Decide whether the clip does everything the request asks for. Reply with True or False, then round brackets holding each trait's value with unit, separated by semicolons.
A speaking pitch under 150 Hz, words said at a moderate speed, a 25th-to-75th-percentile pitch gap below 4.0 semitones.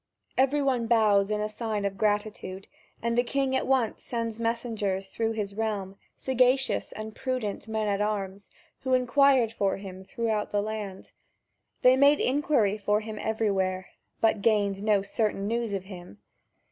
False (215 Hz; 150 wpm; 2.8 semitones)